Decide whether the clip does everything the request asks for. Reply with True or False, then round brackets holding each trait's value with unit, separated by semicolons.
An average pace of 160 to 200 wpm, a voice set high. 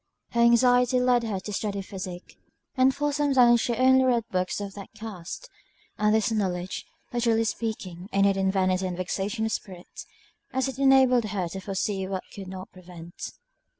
True (180 wpm; 210 Hz)